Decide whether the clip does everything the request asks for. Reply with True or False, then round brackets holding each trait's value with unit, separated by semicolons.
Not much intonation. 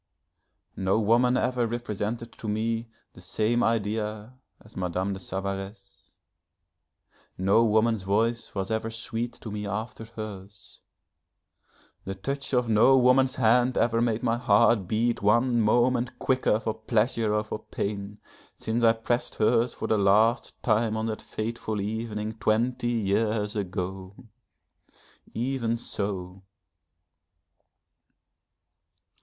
True (2.3 semitones)